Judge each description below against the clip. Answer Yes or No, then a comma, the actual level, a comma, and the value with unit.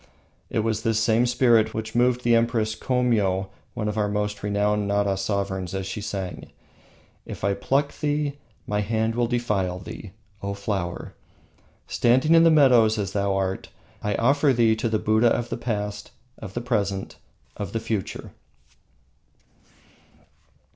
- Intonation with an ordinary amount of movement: Yes, average, 3.0 semitones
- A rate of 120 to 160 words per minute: Yes, average, 155 wpm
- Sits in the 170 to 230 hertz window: No, low, 110 Hz